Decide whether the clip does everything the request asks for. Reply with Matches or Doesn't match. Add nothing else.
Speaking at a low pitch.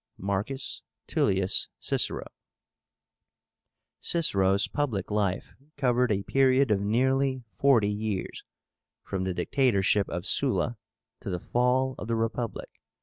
Matches